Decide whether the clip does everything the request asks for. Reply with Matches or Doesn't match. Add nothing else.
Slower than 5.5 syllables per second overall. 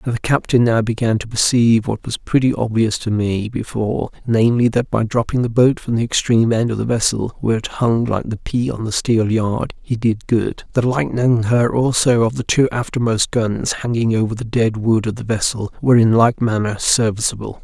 Matches